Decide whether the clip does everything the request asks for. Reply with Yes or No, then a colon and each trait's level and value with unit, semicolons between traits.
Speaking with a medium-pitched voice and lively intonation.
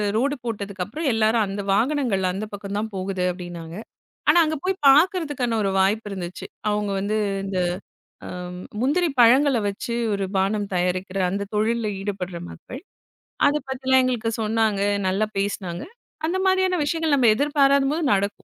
No: high, 215 Hz; wide, 5.8 semitones